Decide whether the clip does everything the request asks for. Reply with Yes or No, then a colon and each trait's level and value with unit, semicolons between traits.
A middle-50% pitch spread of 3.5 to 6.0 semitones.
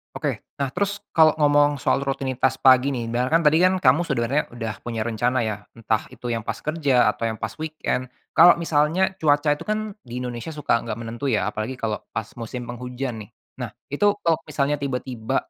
Yes: average, 4.4 semitones